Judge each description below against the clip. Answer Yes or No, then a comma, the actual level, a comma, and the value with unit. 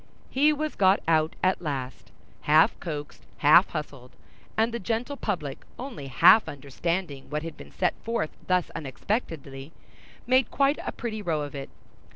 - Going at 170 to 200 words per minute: No, average, 155 wpm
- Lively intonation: Yes, wide, 7.6 semitones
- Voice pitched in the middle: Yes, medium, 165 Hz